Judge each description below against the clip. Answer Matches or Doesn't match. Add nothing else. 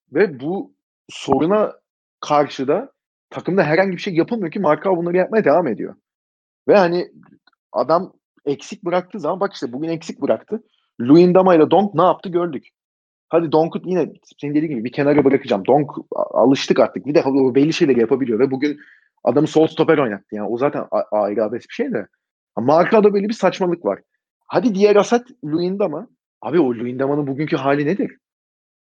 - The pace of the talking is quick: Matches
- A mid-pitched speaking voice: Matches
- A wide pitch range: Doesn't match